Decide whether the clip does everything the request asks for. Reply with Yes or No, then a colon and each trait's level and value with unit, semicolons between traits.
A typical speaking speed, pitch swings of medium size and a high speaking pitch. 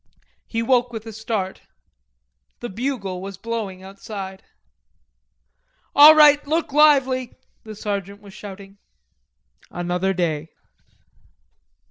No: slow, 100 wpm; average, 4.7 semitones; high, 210 Hz